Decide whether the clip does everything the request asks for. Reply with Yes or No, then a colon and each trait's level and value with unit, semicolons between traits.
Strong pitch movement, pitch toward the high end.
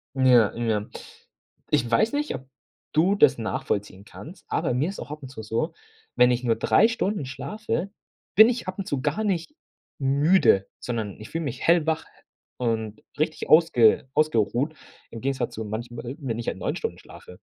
No: wide, 6.2 semitones; low, 130 Hz